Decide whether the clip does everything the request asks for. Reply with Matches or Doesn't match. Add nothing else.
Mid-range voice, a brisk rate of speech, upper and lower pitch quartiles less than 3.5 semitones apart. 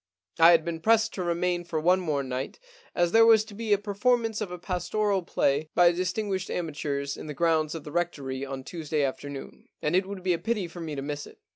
Doesn't match